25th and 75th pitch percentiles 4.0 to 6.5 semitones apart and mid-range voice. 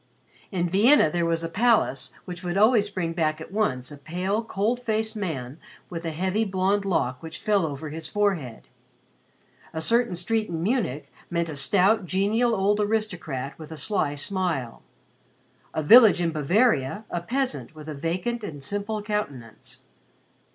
Yes: average, 5.1 semitones; medium, 180 Hz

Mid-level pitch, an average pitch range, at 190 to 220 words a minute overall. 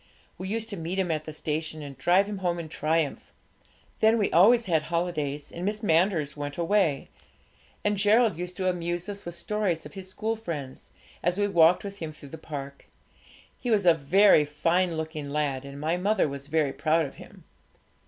Yes: medium, 170 Hz; average, 4.5 semitones; average, 195 wpm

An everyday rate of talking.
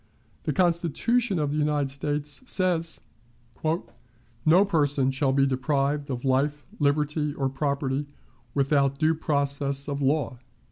No: slow, 125 wpm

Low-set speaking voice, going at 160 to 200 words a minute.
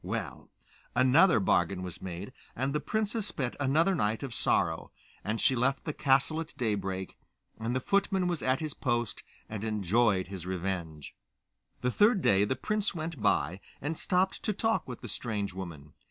Yes: low, 125 Hz; average, 170 wpm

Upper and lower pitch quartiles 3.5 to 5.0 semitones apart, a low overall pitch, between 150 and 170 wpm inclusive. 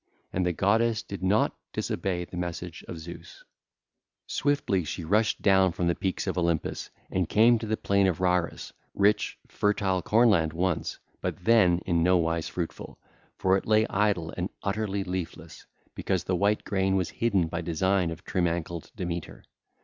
No: average, 2.8 semitones; very low, 95 Hz; average, 165 wpm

